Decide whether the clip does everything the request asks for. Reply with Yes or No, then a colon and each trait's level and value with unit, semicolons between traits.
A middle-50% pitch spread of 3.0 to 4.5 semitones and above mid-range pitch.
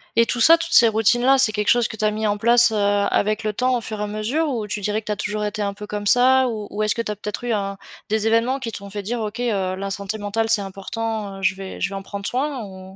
No: narrow, 2.4 semitones; high, 215 Hz